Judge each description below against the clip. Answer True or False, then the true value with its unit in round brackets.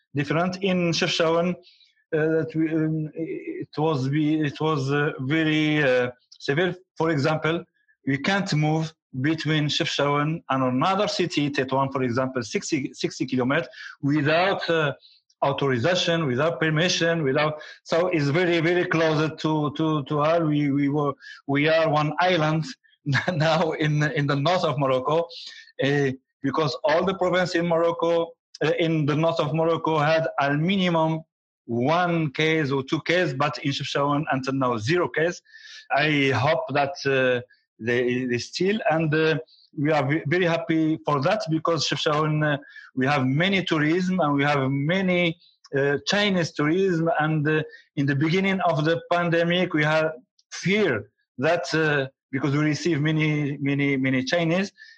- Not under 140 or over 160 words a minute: True (145 wpm)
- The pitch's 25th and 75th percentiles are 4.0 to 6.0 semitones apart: False (2.8 semitones)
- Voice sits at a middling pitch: True (155 Hz)